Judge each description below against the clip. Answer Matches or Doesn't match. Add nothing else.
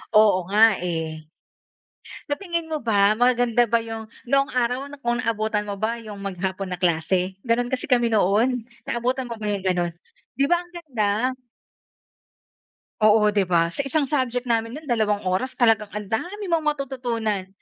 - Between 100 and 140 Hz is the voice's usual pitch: Doesn't match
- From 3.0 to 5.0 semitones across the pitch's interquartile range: Matches